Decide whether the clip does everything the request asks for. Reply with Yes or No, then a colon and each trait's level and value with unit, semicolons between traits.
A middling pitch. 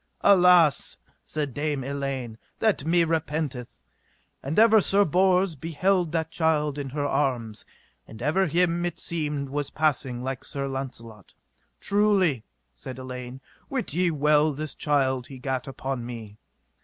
Yes: medium, 145 Hz